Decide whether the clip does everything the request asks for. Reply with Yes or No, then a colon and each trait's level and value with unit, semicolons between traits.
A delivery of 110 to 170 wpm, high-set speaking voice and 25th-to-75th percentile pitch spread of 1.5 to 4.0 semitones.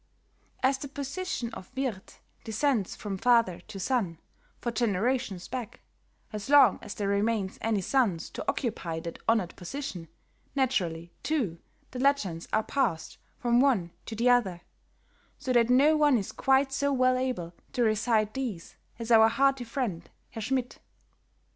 No: average, 150 wpm; high, 230 Hz; average, 5.2 semitones